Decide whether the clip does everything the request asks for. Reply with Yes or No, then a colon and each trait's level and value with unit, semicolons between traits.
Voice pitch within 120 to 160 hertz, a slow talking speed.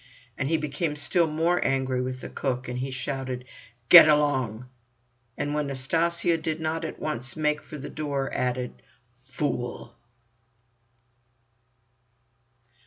Yes: medium, 140 Hz; slow, 120 wpm